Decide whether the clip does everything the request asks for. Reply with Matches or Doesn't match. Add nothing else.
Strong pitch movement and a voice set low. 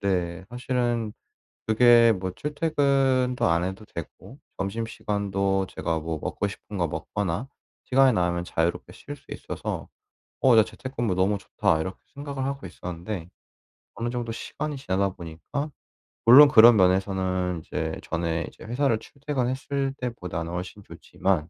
Matches